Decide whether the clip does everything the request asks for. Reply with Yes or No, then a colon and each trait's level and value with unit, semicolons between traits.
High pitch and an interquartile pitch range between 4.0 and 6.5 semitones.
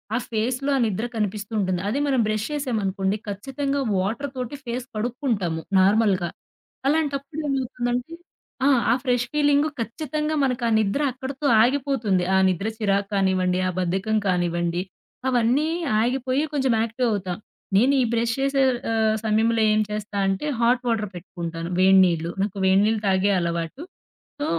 Yes: high, 225 Hz; wide, 5.4 semitones